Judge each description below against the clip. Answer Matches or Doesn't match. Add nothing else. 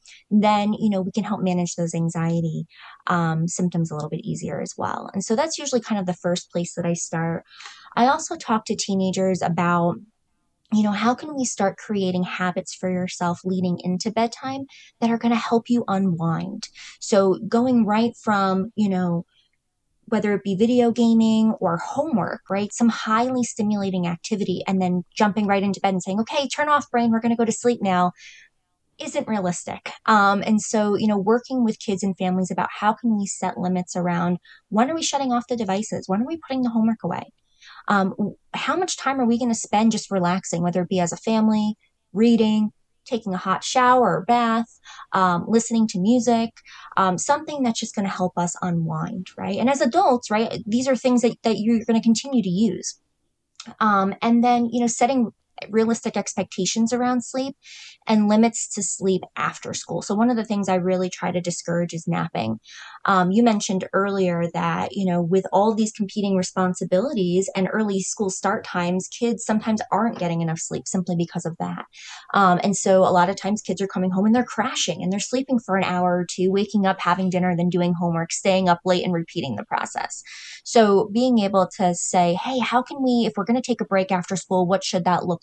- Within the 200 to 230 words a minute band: Matches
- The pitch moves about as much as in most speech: Matches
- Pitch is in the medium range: Doesn't match